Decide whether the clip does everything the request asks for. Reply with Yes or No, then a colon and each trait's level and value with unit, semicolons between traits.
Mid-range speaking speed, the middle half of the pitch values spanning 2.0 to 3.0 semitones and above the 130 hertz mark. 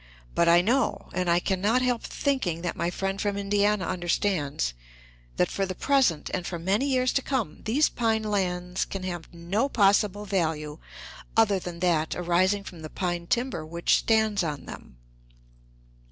No: average, 170 wpm; average, 3.8 semitones; medium, 185 Hz